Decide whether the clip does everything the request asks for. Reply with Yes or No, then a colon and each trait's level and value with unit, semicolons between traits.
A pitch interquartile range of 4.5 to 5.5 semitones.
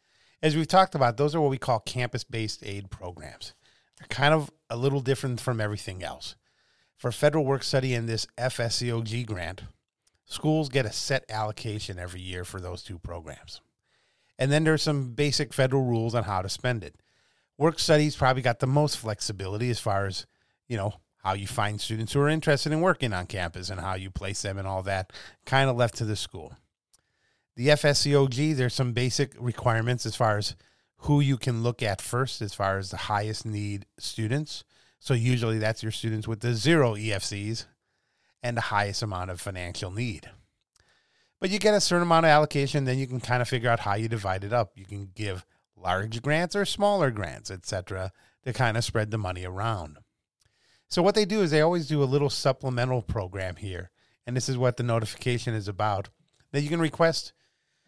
Yes: average, 5.1 semitones